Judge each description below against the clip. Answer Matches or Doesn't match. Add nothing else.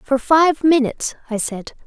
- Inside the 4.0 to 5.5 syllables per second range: Matches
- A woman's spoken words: Matches